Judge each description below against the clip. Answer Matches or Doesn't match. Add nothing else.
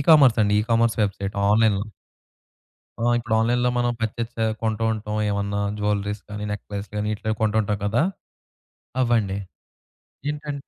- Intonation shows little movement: Matches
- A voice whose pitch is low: Matches